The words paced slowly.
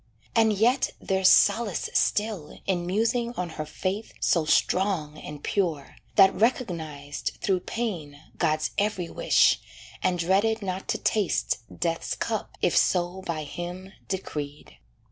Yes: slow, 130 wpm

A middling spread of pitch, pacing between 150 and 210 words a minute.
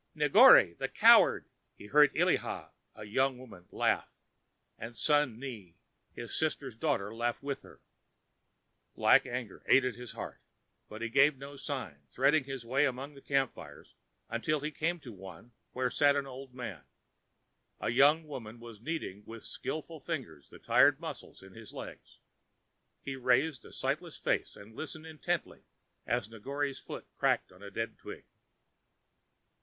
Yes: average, 4.2 semitones; average, 155 wpm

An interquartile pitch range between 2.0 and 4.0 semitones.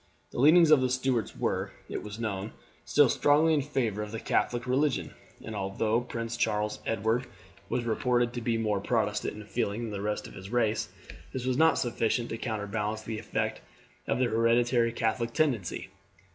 Yes: average, 2.7 semitones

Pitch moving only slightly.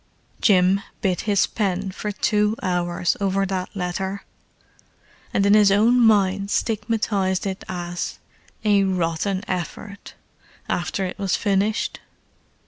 Yes: narrow, 2.0 semitones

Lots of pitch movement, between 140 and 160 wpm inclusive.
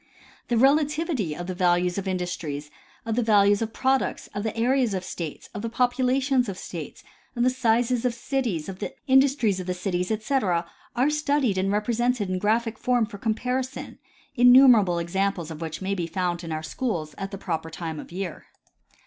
No: wide, 5.7 semitones; average, 185 wpm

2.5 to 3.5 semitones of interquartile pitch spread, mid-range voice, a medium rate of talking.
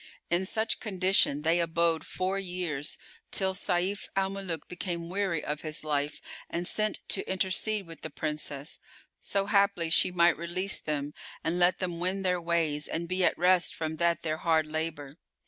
Yes: average, 2.9 semitones; medium, 175 Hz; average, 170 wpm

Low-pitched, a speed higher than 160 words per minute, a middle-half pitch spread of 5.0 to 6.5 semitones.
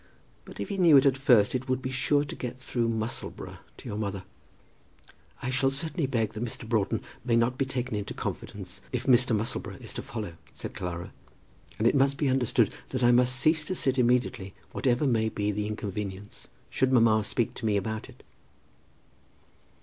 No: low, 120 Hz; average, 190 wpm; average, 3.6 semitones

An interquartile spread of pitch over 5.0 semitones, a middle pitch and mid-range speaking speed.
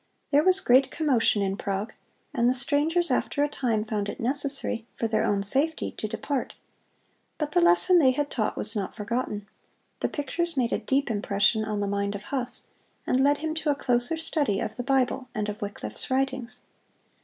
No: wide, 5.4 semitones; high, 245 Hz; average, 190 wpm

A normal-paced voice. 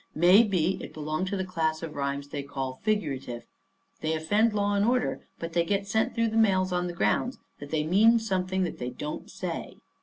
No: fast, 210 wpm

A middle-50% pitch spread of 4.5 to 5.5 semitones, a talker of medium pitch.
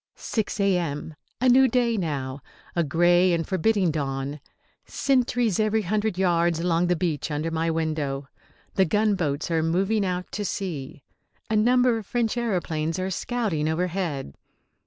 Yes: average, 5.2 semitones; medium, 180 Hz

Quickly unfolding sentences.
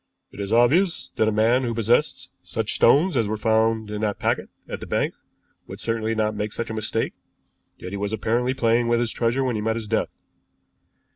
Yes: fast, 210 wpm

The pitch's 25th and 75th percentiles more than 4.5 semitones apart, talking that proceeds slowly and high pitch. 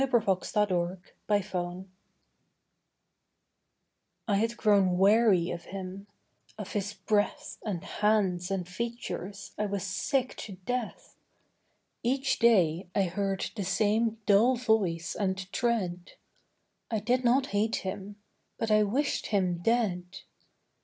No: average, 3.3 semitones; slow, 120 wpm; high, 205 Hz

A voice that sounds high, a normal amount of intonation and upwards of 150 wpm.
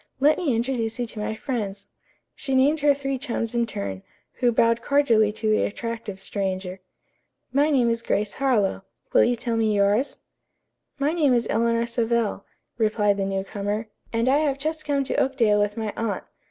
Yes: high, 230 Hz; average, 4.2 semitones; average, 180 wpm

